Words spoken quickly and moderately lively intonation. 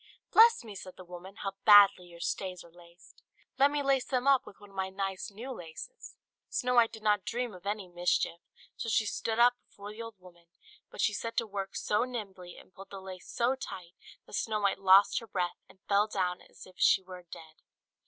Yes: fast, 220 wpm; average, 3.8 semitones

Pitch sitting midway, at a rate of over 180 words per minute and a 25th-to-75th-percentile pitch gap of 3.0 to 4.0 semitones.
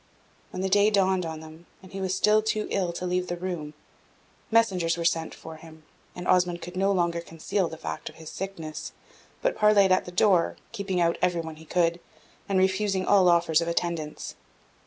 No: medium, 180 Hz; average, 200 wpm; narrow, 2.5 semitones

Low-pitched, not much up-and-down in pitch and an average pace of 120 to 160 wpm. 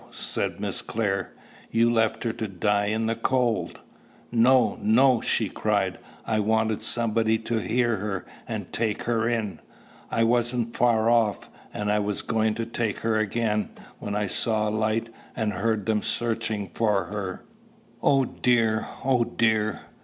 Yes: low, 110 Hz; narrow, 1.6 semitones; average, 155 wpm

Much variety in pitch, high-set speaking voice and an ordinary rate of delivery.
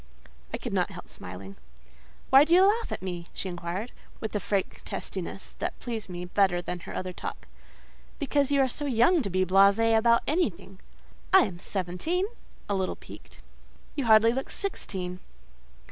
Yes: wide, 6.7 semitones; high, 205 Hz; average, 170 wpm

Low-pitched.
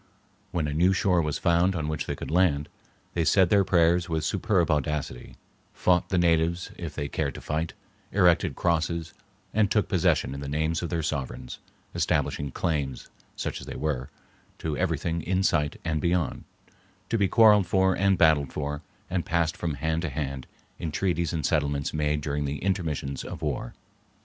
Yes: very low, 80 Hz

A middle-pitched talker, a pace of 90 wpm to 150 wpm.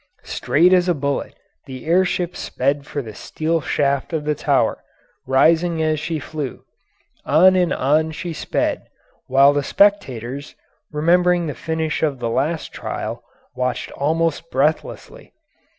Yes: medium, 155 Hz; average, 140 wpm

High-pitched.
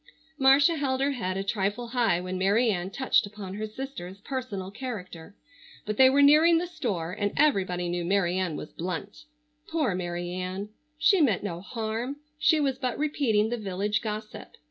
Yes: high, 210 Hz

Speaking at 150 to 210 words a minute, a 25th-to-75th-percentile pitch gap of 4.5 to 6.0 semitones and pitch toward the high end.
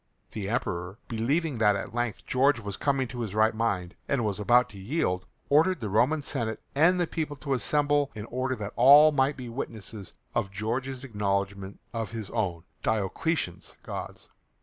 No: average, 170 wpm; average, 5.1 semitones; low, 115 Hz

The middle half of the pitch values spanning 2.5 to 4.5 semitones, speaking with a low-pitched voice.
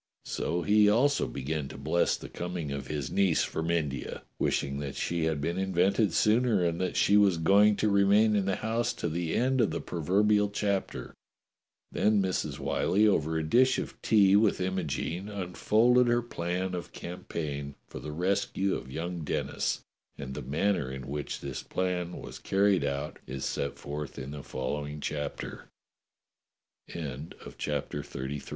No: wide, 5.4 semitones; very low, 90 Hz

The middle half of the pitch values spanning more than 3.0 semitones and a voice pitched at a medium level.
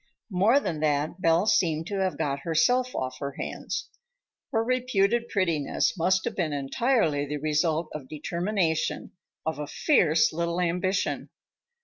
Yes: average, 4.6 semitones; medium, 170 Hz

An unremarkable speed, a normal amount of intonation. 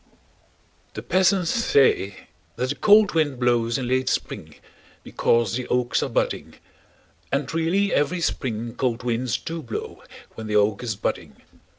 No: average, 150 wpm; wide, 5.8 semitones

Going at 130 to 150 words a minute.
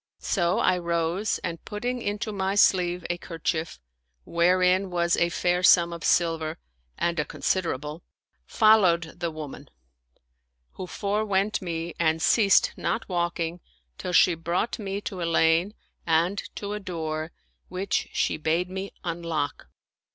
Yes: slow, 135 wpm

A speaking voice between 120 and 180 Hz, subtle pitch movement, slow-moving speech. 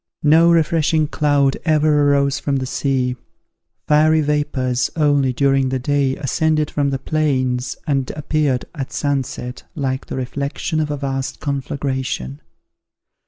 Yes: medium, 140 Hz; narrow, 2.3 semitones; slow, 130 wpm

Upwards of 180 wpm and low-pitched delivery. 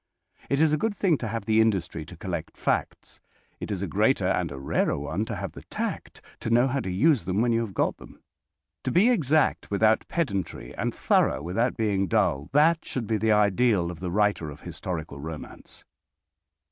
Yes: average, 200 wpm; low, 105 Hz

